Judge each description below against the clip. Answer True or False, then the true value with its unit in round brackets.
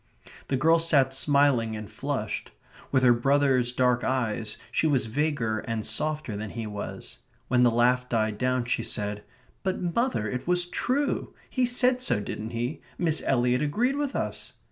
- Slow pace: False (165 wpm)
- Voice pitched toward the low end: True (130 Hz)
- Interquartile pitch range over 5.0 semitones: True (5.4 semitones)